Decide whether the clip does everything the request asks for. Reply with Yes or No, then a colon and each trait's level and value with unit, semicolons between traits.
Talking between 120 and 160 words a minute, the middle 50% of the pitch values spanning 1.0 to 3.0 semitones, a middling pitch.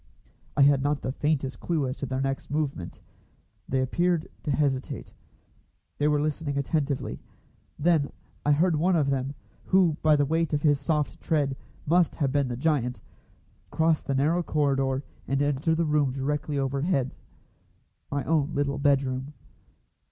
Yes: average, 155 wpm; narrow, 2.4 semitones; medium, 145 Hz